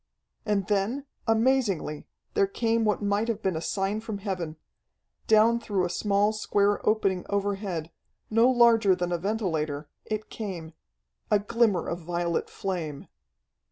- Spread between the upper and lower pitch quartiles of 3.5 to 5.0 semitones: Yes, average, 3.8 semitones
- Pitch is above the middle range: Yes, high, 200 Hz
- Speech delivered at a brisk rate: No, average, 140 wpm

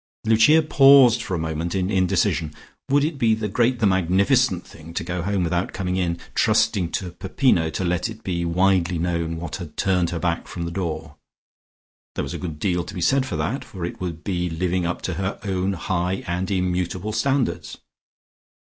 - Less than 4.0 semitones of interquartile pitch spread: Yes, average, 3.6 semitones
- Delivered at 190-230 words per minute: Yes, average, 195 wpm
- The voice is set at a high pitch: No, very low, 90 Hz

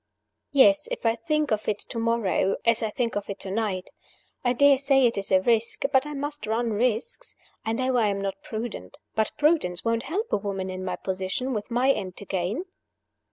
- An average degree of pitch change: Yes, average, 4.9 semitones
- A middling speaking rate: No, fast, 210 wpm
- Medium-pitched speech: No, high, 230 Hz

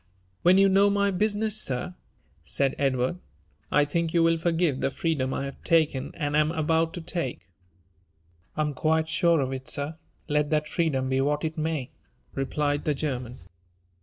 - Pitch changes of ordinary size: Yes, average, 3.4 semitones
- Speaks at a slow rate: No, average, 170 wpm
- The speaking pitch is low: No, medium, 155 Hz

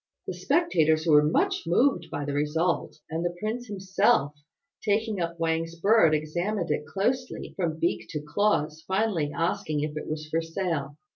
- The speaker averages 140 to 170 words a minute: Yes, average, 160 wpm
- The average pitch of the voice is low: No, medium, 165 Hz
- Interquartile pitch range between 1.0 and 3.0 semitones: No, average, 4.4 semitones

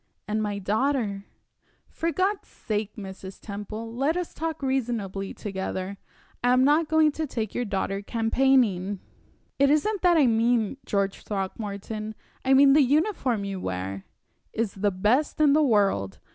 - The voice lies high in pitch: Yes, high, 225 Hz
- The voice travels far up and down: Yes, wide, 5.8 semitones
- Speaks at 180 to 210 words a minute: No, average, 160 wpm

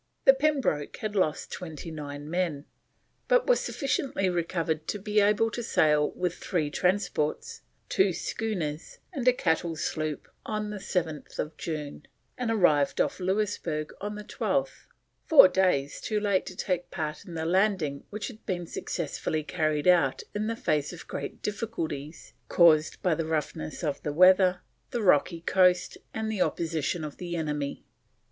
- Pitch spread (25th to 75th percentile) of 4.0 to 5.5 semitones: Yes, average, 5.0 semitones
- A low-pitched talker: No, medium, 175 Hz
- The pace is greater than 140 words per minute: Yes, average, 155 wpm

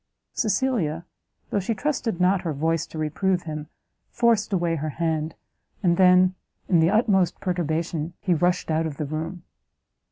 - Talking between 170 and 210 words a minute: No, average, 155 wpm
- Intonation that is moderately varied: Yes, average, 3.2 semitones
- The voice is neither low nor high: Yes, medium, 175 Hz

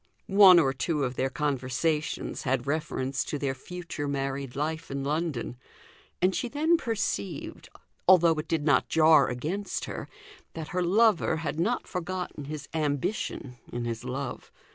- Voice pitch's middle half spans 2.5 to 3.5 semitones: No, average, 4.2 semitones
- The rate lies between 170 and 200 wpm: No, average, 150 wpm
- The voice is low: No, medium, 150 Hz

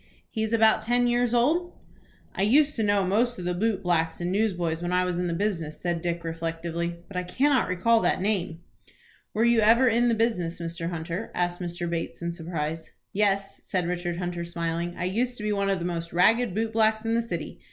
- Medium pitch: Yes, medium, 180 Hz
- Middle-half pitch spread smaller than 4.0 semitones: No, average, 4.6 semitones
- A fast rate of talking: Yes, fast, 215 wpm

